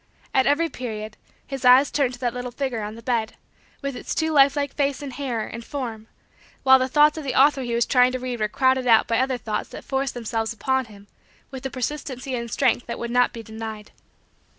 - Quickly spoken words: Yes, fast, 220 wpm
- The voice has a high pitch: Yes, very high, 250 Hz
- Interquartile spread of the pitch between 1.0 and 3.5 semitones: Yes, average, 2.8 semitones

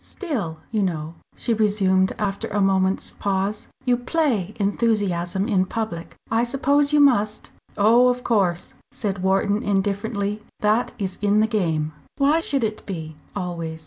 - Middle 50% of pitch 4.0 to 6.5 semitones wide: No, average, 3.4 semitones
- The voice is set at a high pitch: Yes, high, 205 Hz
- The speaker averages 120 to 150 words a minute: Yes, average, 145 wpm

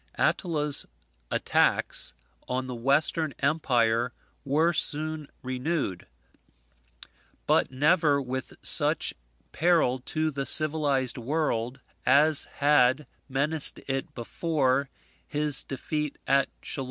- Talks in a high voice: No, medium, 140 Hz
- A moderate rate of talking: No, slow, 95 wpm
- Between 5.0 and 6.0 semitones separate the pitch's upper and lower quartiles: No, average, 3.1 semitones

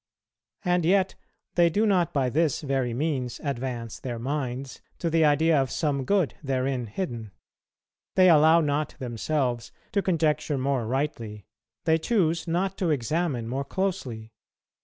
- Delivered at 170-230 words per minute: No, average, 140 wpm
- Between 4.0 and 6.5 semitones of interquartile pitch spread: Yes, average, 4.8 semitones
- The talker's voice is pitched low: No, medium, 145 Hz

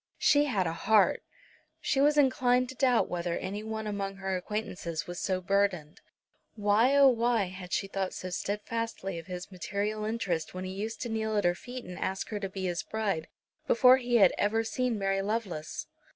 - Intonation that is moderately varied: Yes, average, 3.6 semitones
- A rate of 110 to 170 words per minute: No, average, 195 wpm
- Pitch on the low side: No, high, 205 Hz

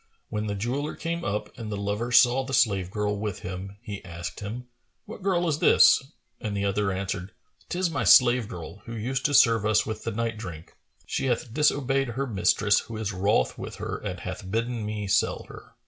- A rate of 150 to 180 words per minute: No, fast, 205 wpm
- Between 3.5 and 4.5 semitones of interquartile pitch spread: Yes, average, 3.8 semitones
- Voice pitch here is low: Yes, low, 110 Hz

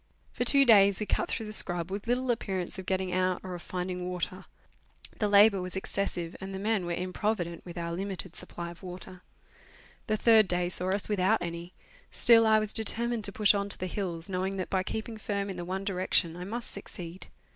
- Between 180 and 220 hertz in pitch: Yes, high, 190 Hz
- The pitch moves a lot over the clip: No, average, 2.8 semitones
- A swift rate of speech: Yes, fast, 210 wpm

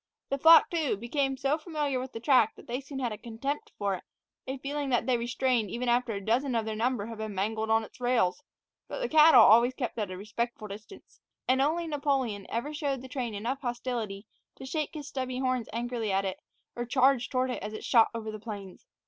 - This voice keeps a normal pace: No, fast, 230 wpm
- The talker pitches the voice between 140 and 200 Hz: No, high, 245 Hz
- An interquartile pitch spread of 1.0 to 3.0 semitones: No, average, 3.6 semitones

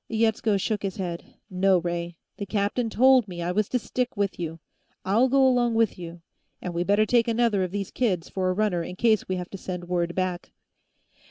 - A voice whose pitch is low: No, high, 195 Hz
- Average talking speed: No, fast, 210 wpm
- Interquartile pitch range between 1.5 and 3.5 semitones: No, average, 4.1 semitones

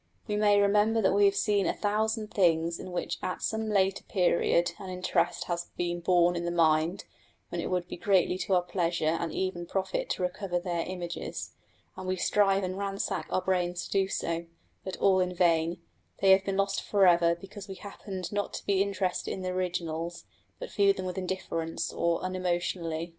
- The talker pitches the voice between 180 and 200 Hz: Yes, medium, 185 Hz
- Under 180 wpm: No, average, 195 wpm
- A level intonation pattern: Yes, narrow, 2.3 semitones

